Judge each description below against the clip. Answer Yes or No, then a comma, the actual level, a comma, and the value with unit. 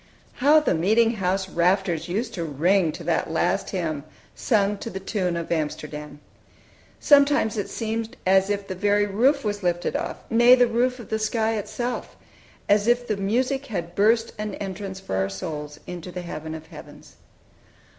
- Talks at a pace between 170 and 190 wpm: Yes, average, 175 wpm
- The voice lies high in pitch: Yes, high, 200 Hz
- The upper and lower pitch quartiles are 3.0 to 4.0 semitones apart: No, average, 4.7 semitones